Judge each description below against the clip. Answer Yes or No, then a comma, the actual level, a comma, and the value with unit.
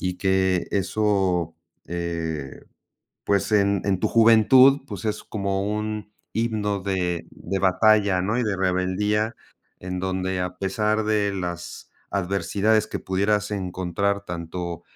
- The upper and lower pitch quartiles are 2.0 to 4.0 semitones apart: Yes, narrow, 2.5 semitones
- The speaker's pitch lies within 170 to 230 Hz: No, low, 100 Hz